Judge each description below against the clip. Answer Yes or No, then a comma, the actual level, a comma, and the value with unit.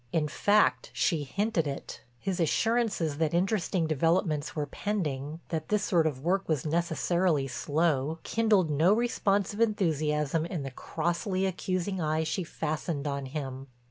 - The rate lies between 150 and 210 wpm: No, average, 140 wpm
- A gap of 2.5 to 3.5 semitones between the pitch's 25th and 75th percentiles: No, average, 4.2 semitones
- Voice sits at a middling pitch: Yes, medium, 165 Hz